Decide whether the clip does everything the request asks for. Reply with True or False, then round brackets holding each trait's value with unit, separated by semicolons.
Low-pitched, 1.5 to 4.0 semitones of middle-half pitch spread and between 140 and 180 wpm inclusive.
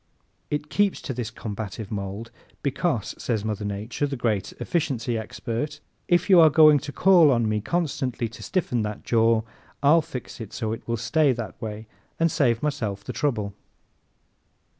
False (120 Hz; 5.3 semitones; 165 wpm)